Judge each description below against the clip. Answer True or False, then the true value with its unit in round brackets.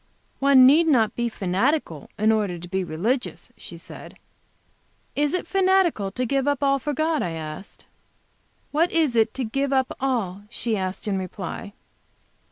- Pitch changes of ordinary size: False (6.5 semitones)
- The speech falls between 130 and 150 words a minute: False (165 wpm)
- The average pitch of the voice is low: False (240 Hz)